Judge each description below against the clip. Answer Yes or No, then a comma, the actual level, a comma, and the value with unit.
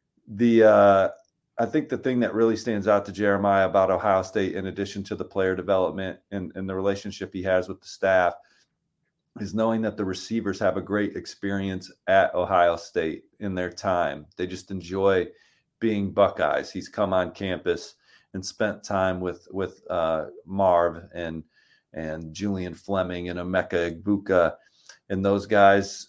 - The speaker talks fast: No, average, 165 wpm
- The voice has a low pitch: Yes, very low, 95 Hz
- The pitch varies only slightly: Yes, narrow, 1.7 semitones